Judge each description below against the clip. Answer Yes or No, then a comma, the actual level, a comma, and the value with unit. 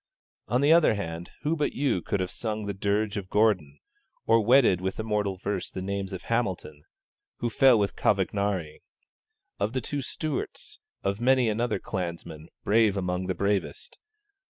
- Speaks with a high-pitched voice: No, low, 100 Hz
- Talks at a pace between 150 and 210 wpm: Yes, average, 160 wpm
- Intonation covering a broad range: No, average, 3.8 semitones